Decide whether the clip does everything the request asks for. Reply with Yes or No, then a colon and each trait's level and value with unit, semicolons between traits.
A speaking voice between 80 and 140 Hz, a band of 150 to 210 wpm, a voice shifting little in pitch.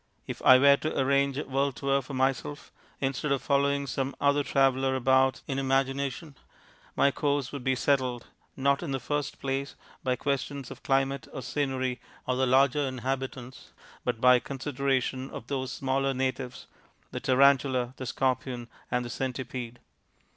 Yes: low, 135 Hz; average, 155 wpm; narrow, 1.3 semitones